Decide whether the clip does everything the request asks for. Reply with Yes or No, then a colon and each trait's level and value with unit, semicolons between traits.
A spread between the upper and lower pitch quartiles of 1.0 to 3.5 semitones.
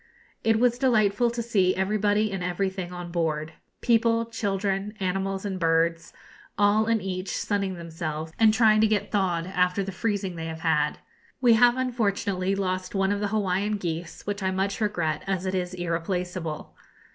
Yes: average, 3.0 semitones